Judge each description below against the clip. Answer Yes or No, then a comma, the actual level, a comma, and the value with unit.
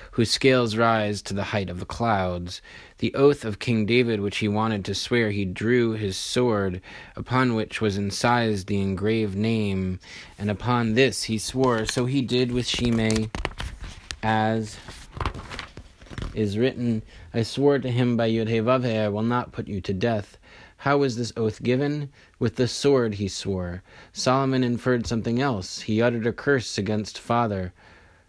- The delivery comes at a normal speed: Yes, average, 160 wpm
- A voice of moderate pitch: No, low, 110 Hz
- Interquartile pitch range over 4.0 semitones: No, average, 3.4 semitones